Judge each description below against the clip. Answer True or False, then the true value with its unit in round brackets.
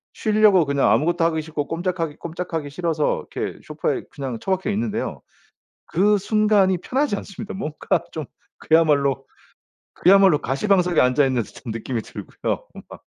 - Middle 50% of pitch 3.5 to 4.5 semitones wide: False (5.2 semitones)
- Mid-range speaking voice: True (170 Hz)